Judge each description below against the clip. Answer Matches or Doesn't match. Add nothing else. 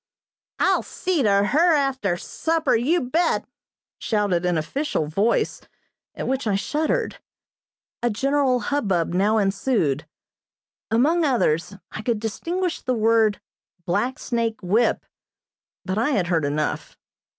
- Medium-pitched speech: Doesn't match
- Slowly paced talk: Matches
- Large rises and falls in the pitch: Matches